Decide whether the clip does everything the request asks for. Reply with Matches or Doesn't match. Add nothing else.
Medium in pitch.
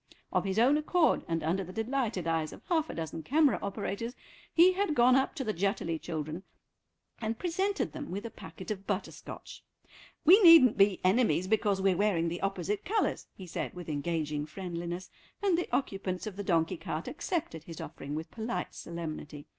Doesn't match